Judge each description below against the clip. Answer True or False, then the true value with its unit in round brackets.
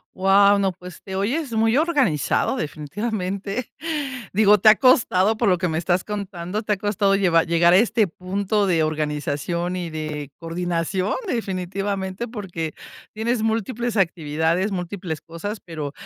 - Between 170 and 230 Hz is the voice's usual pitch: True (190 Hz)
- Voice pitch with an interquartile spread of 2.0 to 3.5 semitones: False (3.9 semitones)